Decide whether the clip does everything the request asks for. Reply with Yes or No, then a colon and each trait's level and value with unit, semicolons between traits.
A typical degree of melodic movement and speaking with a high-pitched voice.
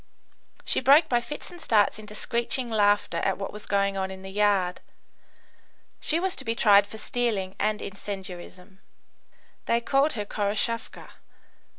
Yes: average, 3.3 semitones; high, 210 Hz